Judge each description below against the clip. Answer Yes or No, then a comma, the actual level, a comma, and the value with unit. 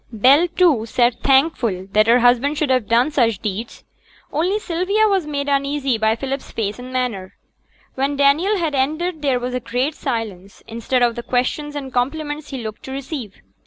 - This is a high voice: Yes, very high, 265 Hz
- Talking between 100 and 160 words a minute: No, average, 180 wpm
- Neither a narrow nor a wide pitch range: Yes, average, 4.1 semitones